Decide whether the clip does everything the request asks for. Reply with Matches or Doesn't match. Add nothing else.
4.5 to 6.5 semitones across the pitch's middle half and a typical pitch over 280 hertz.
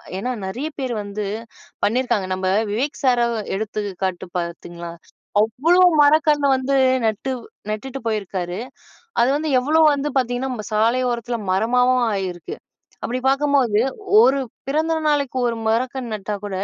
Doesn't match